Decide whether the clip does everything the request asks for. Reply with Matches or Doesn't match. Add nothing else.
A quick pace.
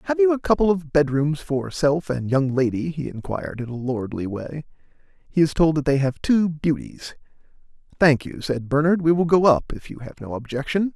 Matches